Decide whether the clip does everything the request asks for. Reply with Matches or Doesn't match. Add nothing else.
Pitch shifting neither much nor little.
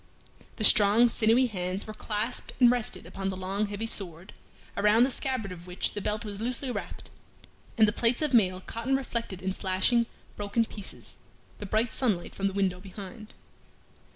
Matches